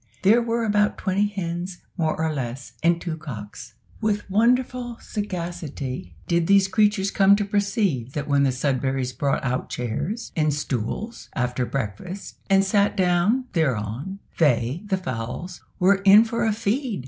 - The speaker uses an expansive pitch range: Yes, wide, 7.4 semitones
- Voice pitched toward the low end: No, medium, 175 Hz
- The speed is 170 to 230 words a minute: No, average, 150 wpm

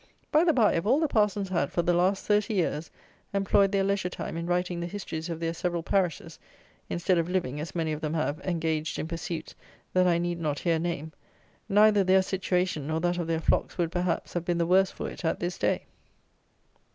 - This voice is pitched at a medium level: Yes, medium, 175 Hz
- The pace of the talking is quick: Yes, fast, 215 wpm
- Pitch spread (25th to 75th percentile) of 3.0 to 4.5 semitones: No, narrow, 2.5 semitones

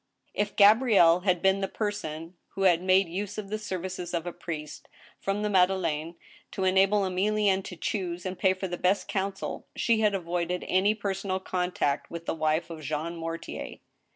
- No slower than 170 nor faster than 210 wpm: Yes, average, 180 wpm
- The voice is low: No, medium, 185 Hz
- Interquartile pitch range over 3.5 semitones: No, narrow, 2.6 semitones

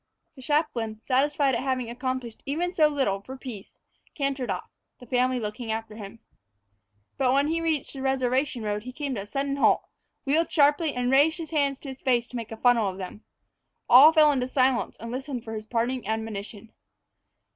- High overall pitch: Yes, very high, 255 Hz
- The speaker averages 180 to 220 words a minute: Yes, average, 190 wpm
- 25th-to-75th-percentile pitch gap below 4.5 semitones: Yes, average, 3.6 semitones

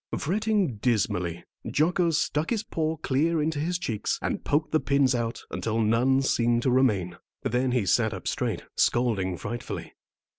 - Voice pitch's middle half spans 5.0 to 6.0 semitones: Yes, wide, 5.6 semitones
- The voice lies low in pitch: Yes, low, 130 Hz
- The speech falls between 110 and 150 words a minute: No, average, 160 wpm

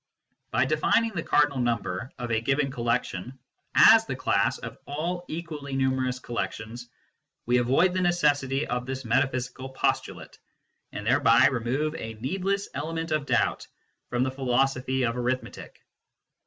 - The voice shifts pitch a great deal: No, average, 3.4 semitones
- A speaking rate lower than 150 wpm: Yes, average, 140 wpm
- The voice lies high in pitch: No, low, 130 Hz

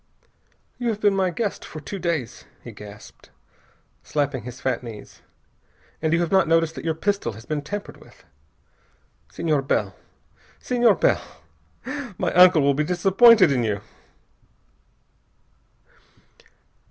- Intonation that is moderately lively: No, wide, 6.0 semitones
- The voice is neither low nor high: Yes, medium, 165 Hz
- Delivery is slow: Yes, slow, 130 wpm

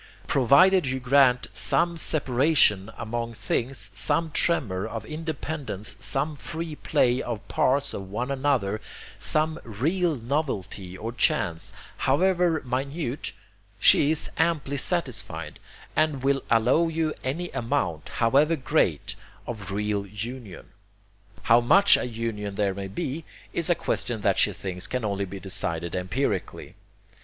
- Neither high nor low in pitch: No, low, 125 Hz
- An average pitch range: No, wide, 6.8 semitones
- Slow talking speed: Yes, slow, 130 wpm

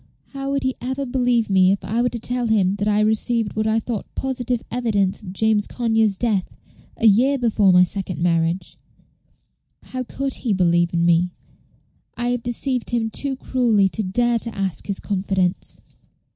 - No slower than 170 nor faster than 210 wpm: Yes, average, 180 wpm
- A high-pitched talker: Yes, high, 220 Hz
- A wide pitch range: No, average, 4.1 semitones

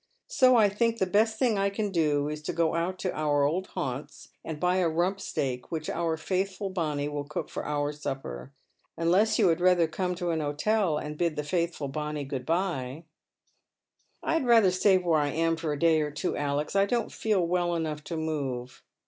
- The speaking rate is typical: No, fast, 210 wpm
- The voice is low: No, medium, 165 Hz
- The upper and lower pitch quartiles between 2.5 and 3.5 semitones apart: No, average, 4.1 semitones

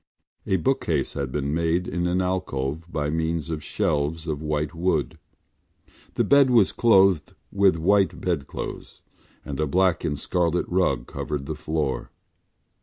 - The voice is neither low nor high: No, very low, 80 Hz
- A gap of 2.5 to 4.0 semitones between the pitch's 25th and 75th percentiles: Yes, average, 3.7 semitones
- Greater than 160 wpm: No, average, 145 wpm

